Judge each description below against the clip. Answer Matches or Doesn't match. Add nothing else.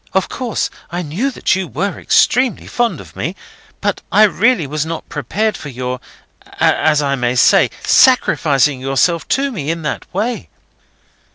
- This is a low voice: Doesn't match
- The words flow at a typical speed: Matches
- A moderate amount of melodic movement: Doesn't match